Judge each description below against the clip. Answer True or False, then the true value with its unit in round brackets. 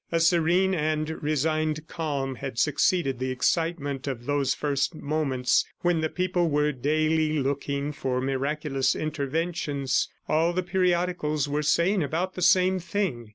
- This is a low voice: False (155 Hz)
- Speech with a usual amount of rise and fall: True (3.4 semitones)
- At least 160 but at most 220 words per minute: False (140 wpm)